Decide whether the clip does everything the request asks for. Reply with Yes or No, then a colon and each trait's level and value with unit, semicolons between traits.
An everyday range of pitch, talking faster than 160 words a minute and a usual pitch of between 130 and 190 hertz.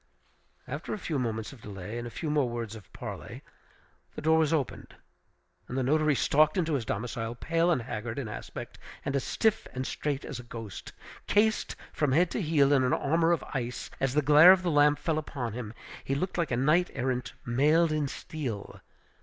Yes: average, 4.6 semitones; fast, 205 wpm; medium, 140 Hz